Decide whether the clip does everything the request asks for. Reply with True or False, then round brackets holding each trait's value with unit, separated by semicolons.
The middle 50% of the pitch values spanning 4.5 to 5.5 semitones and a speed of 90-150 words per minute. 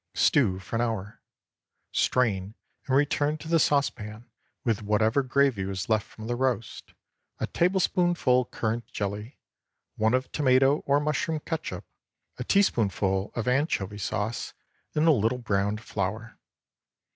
True (5.1 semitones; 135 wpm)